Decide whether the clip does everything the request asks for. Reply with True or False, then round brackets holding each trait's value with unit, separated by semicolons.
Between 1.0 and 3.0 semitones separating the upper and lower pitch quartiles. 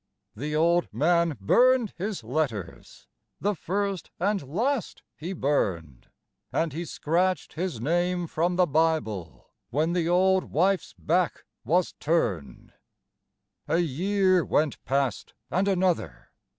False (4.4 semitones)